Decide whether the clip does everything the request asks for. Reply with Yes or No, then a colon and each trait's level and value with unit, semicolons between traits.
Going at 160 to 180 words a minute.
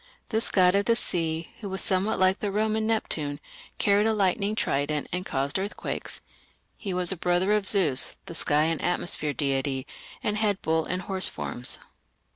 Yes: average, 175 wpm